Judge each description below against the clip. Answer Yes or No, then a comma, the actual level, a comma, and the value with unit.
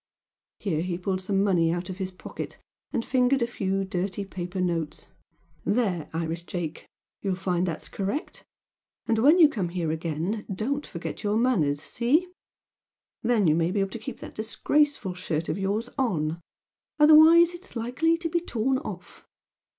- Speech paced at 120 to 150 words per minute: No, average, 165 wpm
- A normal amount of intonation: No, wide, 6.0 semitones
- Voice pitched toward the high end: Yes, high, 195 Hz